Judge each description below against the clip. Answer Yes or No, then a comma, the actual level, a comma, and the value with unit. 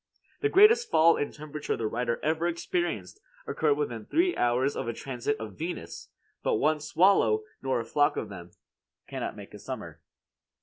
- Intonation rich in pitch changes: Yes, wide, 6.3 semitones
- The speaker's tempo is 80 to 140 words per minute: No, average, 170 wpm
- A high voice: No, medium, 145 Hz